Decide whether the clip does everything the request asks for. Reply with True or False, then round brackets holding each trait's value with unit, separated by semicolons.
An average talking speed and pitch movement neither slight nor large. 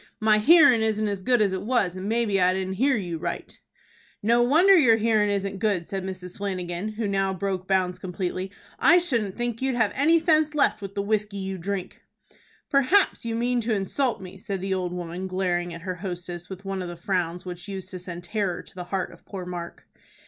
False (215 wpm; 3.7 semitones)